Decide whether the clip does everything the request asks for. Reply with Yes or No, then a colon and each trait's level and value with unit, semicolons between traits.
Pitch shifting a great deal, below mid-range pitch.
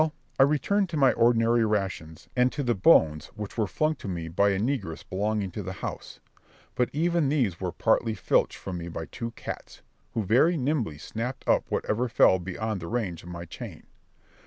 Yes: wide, 5.7 semitones; low, 110 Hz